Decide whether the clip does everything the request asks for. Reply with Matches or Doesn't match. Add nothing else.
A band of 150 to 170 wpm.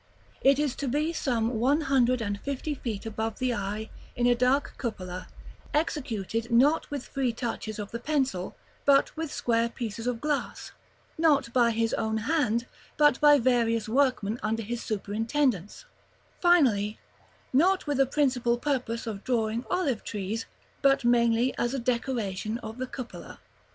Matches